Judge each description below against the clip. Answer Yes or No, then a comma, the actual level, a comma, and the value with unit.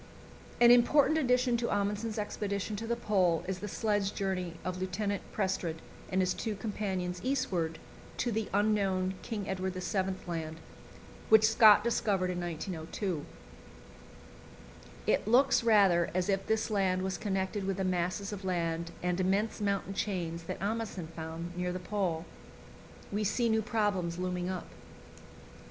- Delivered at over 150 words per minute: No, average, 145 wpm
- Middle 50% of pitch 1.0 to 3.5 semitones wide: Yes, average, 2.9 semitones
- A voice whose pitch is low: No, high, 195 Hz